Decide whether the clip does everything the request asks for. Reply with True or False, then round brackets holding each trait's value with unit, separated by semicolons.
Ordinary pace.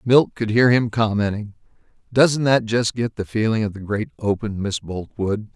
True (185 wpm)